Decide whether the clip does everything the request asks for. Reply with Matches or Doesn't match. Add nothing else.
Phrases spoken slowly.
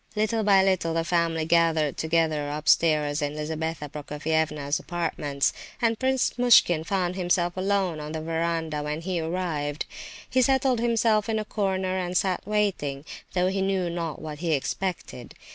Doesn't match